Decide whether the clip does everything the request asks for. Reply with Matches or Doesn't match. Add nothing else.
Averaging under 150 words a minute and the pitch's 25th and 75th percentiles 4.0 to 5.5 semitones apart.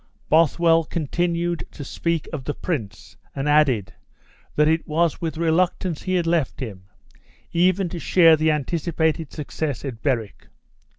Doesn't match